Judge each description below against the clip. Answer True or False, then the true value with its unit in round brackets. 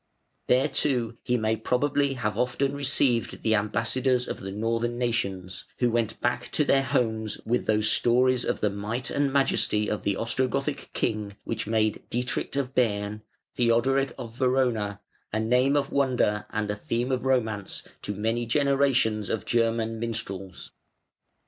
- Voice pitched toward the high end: False (115 Hz)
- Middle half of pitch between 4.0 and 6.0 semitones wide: False (3.1 semitones)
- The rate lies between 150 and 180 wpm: True (155 wpm)